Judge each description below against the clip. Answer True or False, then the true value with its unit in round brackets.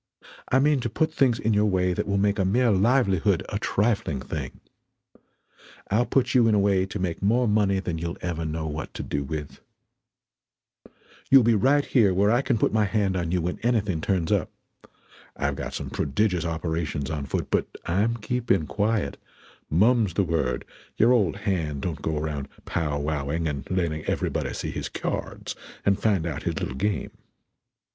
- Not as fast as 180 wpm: False (185 wpm)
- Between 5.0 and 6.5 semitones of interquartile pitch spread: True (5.3 semitones)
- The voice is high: False (95 Hz)